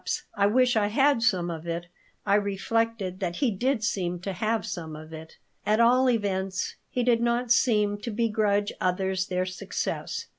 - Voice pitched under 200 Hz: No, high, 205 Hz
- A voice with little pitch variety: No, average, 3.9 semitones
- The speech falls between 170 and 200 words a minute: Yes, average, 175 wpm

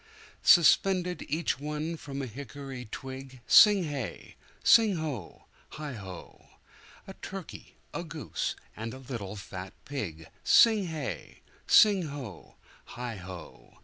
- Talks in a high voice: No, medium, 140 Hz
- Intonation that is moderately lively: No, wide, 6.9 semitones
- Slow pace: Yes, slow, 110 wpm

